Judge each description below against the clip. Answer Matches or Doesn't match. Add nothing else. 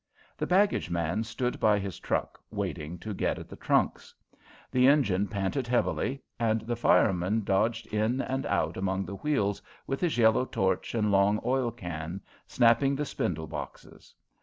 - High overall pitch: Doesn't match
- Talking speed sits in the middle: Matches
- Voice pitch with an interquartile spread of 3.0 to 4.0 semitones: Doesn't match